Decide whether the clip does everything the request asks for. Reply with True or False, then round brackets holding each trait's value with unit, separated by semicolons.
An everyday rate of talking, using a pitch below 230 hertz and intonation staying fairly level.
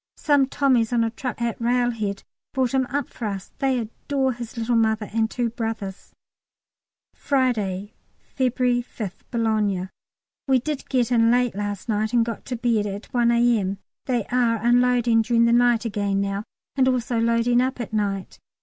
False (170 wpm; 235 Hz; 2.3 semitones)